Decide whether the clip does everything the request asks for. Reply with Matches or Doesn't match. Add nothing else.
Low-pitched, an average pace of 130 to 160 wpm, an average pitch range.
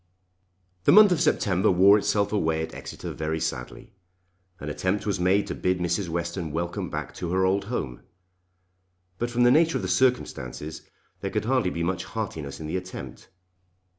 Doesn't match